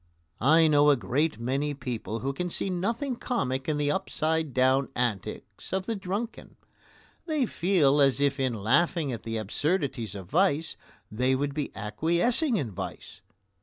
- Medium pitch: Yes, medium, 145 Hz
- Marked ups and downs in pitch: Yes, wide, 5.8 semitones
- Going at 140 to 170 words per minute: Yes, average, 160 wpm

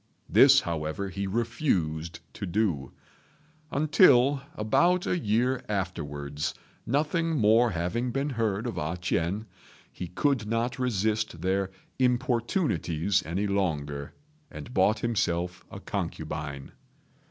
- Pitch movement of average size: No, wide, 6.3 semitones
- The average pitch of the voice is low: Yes, low, 105 Hz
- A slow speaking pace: Yes, slow, 110 wpm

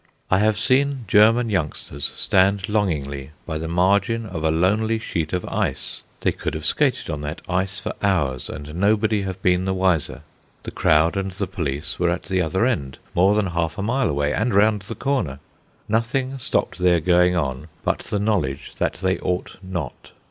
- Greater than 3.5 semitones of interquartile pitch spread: Yes, average, 4.8 semitones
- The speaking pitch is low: Yes, very low, 95 Hz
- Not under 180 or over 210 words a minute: Yes, average, 185 wpm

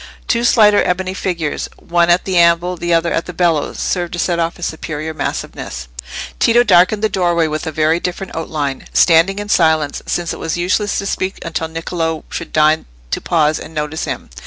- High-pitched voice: No, medium, 170 Hz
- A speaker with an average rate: Yes, average, 195 wpm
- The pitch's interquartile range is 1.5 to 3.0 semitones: Yes, narrow, 2.4 semitones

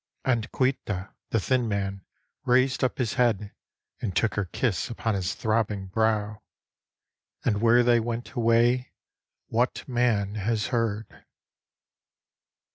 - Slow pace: Yes, slow, 120 wpm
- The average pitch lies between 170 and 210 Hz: No, low, 115 Hz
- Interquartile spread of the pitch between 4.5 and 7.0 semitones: No, average, 2.8 semitones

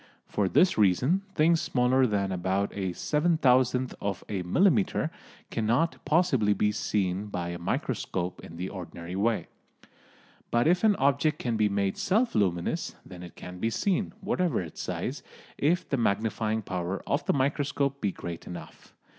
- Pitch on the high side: No, low, 110 Hz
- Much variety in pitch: Yes, wide, 7.5 semitones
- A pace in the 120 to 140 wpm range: No, average, 160 wpm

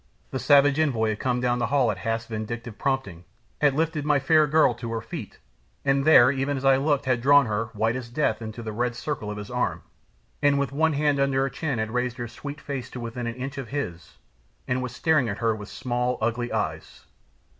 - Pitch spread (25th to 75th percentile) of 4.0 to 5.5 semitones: No, average, 3.5 semitones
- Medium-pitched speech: No, low, 125 Hz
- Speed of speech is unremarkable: No, fast, 225 wpm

